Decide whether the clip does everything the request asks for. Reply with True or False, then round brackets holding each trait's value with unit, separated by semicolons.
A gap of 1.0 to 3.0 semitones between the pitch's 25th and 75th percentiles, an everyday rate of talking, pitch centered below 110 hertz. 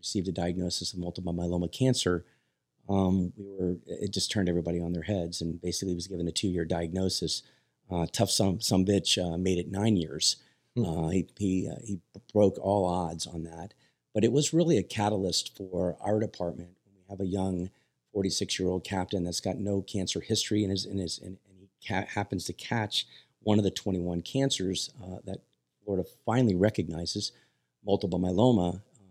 True (2.6 semitones; 180 wpm; 95 Hz)